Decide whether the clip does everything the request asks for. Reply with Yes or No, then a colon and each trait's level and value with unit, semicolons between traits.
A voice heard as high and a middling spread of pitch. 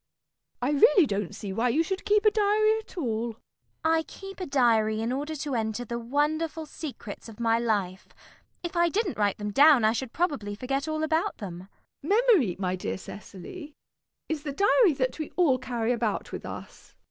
No: very high, 275 Hz; wide, 6.7 semitones